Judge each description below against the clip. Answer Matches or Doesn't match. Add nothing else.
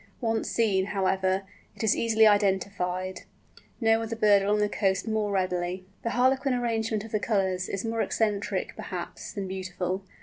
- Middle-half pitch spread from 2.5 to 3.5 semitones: Matches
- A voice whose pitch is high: Matches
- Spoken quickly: Doesn't match